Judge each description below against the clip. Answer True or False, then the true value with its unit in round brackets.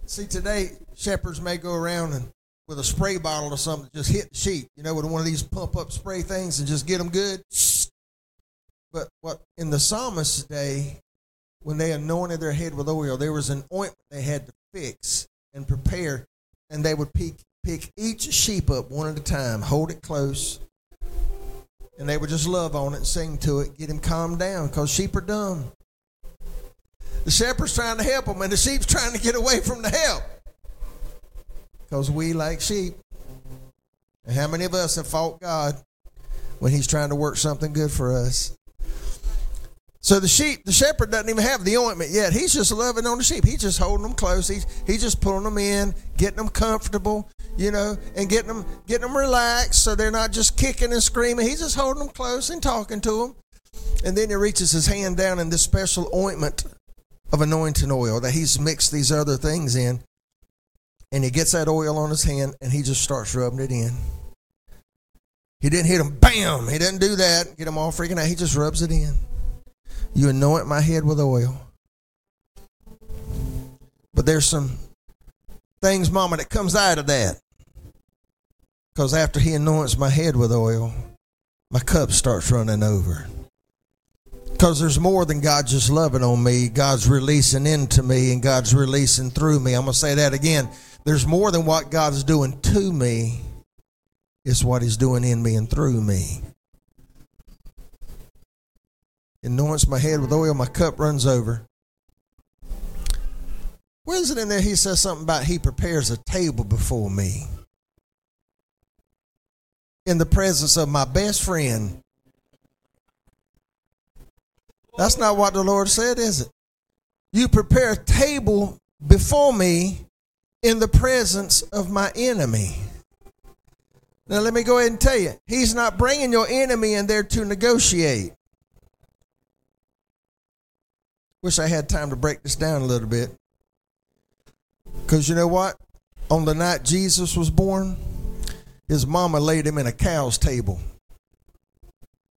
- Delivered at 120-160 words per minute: False (170 wpm)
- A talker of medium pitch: True (155 Hz)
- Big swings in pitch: True (6.6 semitones)